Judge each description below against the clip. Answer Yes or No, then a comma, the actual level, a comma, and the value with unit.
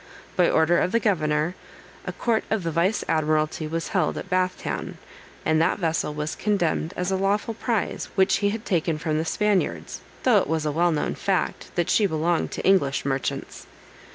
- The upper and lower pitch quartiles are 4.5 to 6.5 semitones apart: No, average, 3.9 semitones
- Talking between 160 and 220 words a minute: Yes, average, 185 wpm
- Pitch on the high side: No, medium, 170 Hz